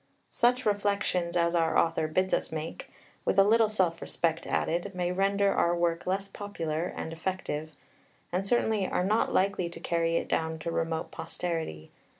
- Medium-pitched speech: Yes, medium, 175 Hz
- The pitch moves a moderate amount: Yes, average, 3.2 semitones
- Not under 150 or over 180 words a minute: Yes, average, 165 wpm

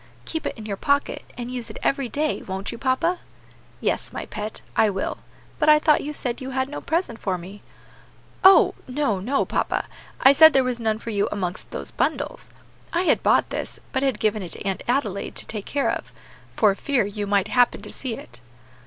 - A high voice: Yes, high, 240 Hz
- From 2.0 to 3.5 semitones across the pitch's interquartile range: No, average, 5.3 semitones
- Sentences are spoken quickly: Yes, fast, 210 wpm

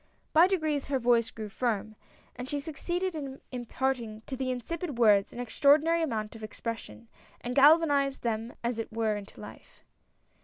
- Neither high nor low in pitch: No, very high, 250 Hz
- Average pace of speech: Yes, average, 185 wpm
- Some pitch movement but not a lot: Yes, average, 4.5 semitones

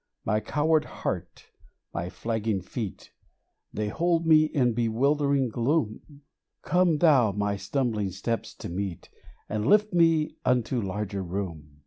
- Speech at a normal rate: No, slow, 125 wpm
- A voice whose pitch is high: No, low, 115 Hz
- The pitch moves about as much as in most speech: No, wide, 6.8 semitones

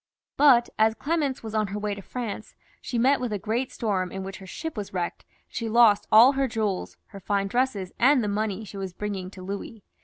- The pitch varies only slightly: No, average, 3.5 semitones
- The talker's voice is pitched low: No, high, 215 Hz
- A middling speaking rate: No, fast, 225 wpm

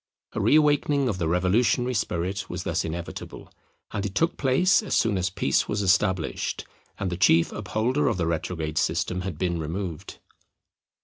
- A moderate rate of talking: Yes, average, 170 wpm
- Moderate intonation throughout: No, wide, 5.8 semitones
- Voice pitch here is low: Yes, very low, 95 Hz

